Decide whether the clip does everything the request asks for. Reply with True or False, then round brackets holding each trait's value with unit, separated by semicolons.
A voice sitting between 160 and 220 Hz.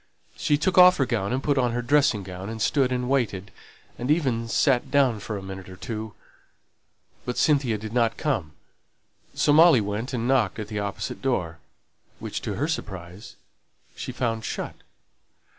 False (120 Hz)